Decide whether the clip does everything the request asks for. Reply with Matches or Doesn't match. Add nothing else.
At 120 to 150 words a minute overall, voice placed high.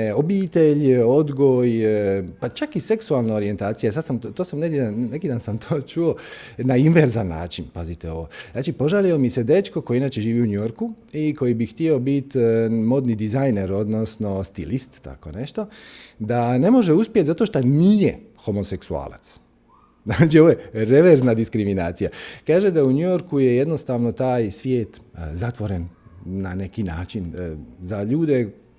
Doesn't match